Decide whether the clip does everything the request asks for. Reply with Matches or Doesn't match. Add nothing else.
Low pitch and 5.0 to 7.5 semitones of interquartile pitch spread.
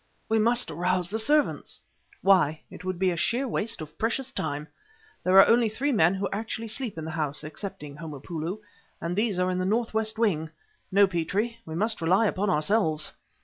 Doesn't match